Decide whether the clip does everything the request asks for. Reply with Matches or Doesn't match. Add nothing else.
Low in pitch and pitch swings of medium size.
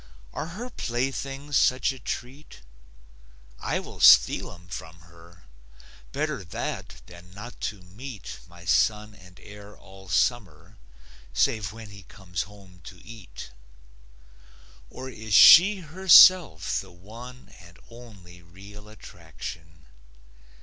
Doesn't match